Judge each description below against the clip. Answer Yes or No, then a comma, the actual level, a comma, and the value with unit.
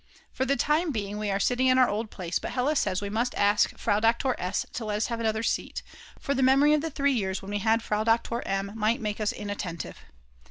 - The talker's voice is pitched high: Yes, high, 225 Hz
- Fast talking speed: Yes, fast, 245 wpm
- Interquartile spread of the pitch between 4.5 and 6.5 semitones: No, average, 3.9 semitones